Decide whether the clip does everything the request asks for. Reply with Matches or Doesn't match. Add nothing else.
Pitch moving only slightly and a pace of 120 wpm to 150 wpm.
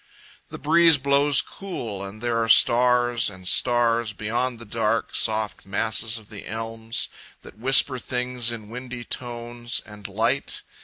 Matches